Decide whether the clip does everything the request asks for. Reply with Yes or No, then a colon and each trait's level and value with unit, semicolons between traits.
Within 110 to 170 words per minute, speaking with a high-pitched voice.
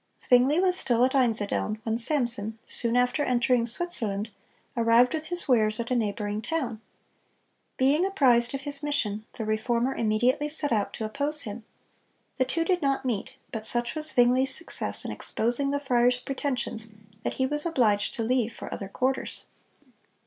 Yes: average, 165 wpm; high, 245 Hz